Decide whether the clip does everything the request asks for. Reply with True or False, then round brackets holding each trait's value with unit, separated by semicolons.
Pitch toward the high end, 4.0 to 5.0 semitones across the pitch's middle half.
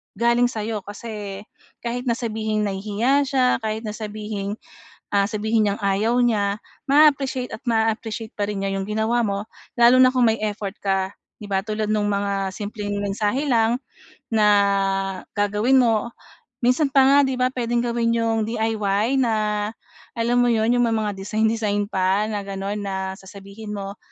False (220 Hz; 2.7 semitones)